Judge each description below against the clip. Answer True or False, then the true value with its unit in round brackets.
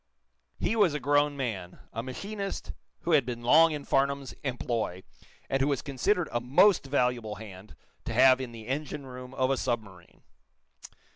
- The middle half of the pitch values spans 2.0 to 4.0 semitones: True (3.6 semitones)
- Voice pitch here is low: True (130 Hz)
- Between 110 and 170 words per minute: True (165 wpm)